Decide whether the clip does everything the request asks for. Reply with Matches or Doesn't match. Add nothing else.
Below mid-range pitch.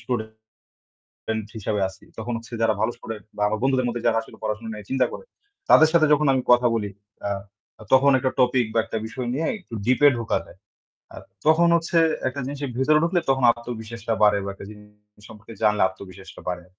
Matches